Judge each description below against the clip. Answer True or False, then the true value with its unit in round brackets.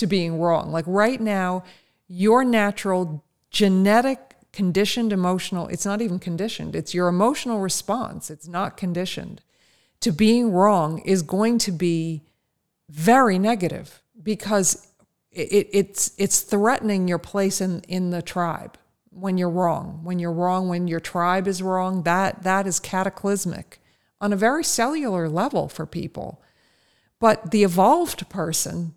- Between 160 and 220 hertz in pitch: True (190 Hz)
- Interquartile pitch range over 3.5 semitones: False (2.9 semitones)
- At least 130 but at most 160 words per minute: True (140 wpm)